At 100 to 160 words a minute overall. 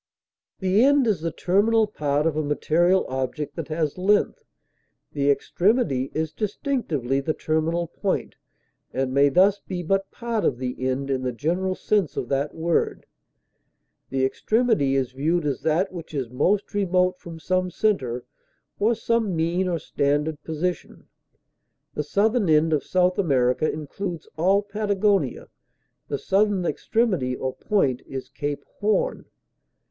Yes: average, 145 wpm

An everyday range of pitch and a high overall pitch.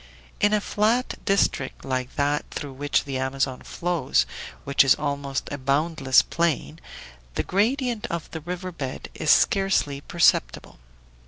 No: average, 4.9 semitones; medium, 145 Hz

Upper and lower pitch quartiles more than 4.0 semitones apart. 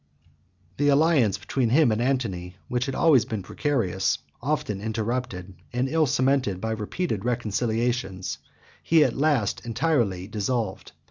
Yes: average, 4.9 semitones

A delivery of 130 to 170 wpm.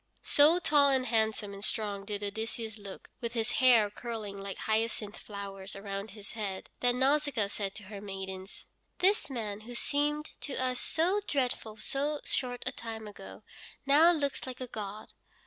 Yes: average, 165 wpm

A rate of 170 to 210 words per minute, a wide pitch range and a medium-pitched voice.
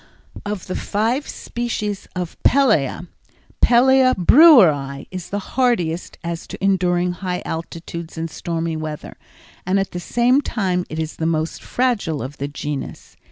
No: average, 145 wpm; wide, 6.0 semitones; medium, 180 Hz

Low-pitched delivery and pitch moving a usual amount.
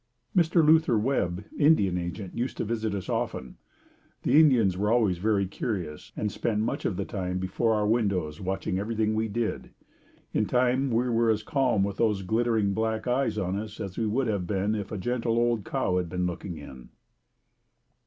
Yes: low, 105 Hz; average, 3.7 semitones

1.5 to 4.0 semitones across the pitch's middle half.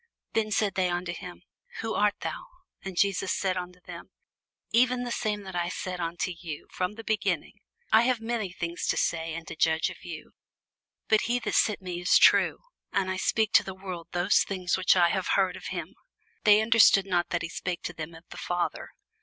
Yes: average, 3.2 semitones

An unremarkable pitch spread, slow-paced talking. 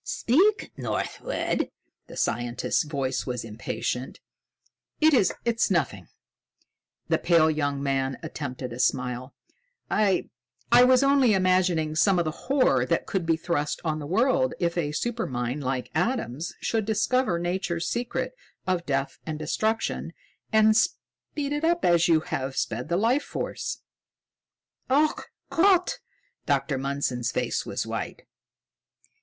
No: wide, 8.7 semitones; slow, 130 wpm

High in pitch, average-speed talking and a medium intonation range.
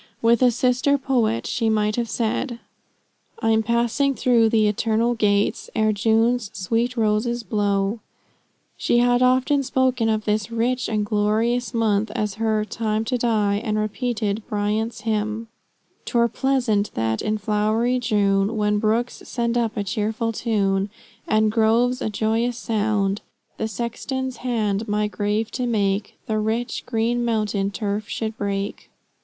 No: high, 220 Hz; average, 145 wpm; narrow, 2.1 semitones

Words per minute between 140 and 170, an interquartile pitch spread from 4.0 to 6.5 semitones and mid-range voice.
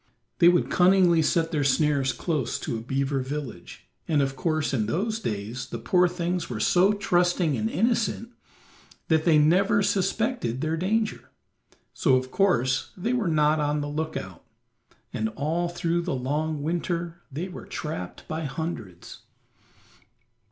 Yes: average, 150 wpm; average, 4.8 semitones; medium, 160 Hz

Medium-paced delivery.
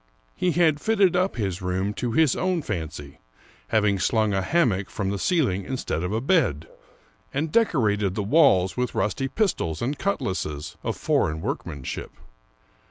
Yes: average, 160 wpm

